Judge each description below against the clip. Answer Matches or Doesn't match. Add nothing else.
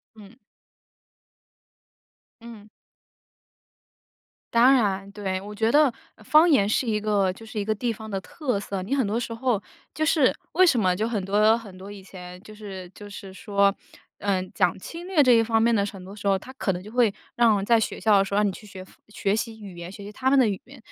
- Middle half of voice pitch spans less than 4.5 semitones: Matches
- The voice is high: Matches